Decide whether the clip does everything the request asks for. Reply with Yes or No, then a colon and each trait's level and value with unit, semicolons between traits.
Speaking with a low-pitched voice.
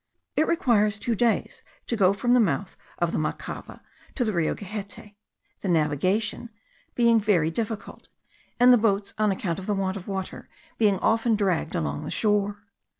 No: high, 205 Hz